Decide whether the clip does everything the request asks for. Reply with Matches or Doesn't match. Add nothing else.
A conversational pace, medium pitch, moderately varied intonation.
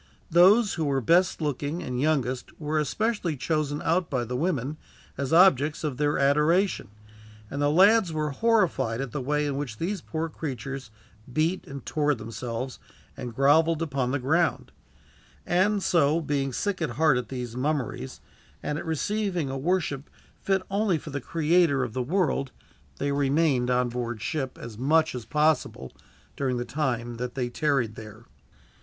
Matches